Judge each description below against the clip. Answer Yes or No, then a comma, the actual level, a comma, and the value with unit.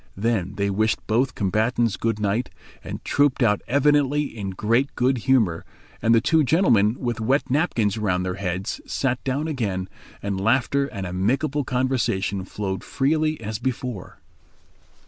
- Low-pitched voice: Yes, low, 115 Hz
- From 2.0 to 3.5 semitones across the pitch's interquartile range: No, average, 5.0 semitones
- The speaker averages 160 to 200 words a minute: No, average, 145 wpm